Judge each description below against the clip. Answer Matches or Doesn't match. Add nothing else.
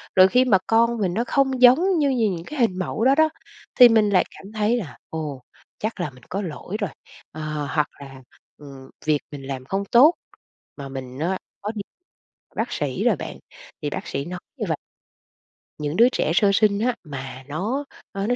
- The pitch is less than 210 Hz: Matches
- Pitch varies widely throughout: Matches